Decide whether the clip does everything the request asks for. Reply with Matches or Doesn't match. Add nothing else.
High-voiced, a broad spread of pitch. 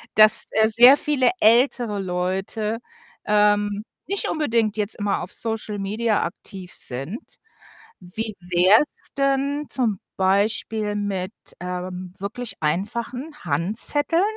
Doesn't match